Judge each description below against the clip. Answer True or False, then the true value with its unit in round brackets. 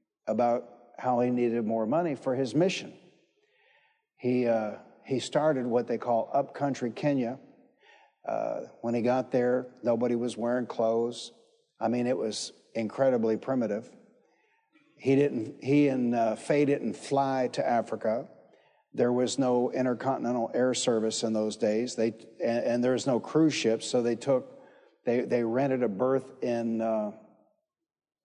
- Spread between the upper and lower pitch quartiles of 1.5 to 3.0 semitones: True (2.6 semitones)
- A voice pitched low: True (125 Hz)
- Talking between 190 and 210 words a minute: False (150 wpm)